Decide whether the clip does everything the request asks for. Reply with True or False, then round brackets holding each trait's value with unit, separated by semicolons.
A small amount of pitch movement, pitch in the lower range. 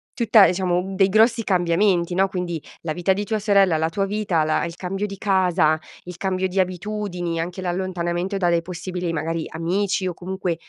False (2.2 semitones; 185 Hz)